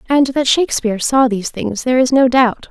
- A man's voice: No, female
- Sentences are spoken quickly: Yes, fast, 220 wpm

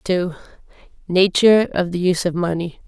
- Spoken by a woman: Yes, female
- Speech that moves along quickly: No, average, 145 wpm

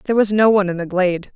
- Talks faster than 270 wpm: Yes, fast, 310 wpm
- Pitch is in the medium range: No, high, 195 Hz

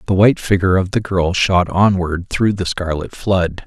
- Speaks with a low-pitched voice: Yes, very low, 95 Hz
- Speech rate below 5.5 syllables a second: Yes, 4.9 syllables/s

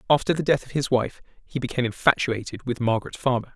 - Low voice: Yes, low, 125 Hz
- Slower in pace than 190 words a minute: No, average, 200 wpm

